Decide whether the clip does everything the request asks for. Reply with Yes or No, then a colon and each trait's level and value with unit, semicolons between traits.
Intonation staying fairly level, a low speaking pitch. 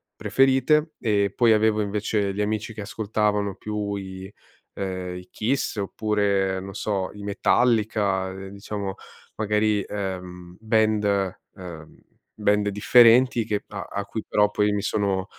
Yes: narrow, 1.8 semitones; low, 105 Hz